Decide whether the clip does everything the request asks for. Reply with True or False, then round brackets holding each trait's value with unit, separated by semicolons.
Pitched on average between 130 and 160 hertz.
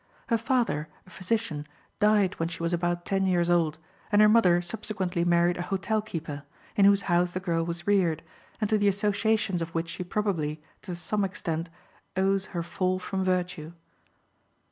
False (180 Hz)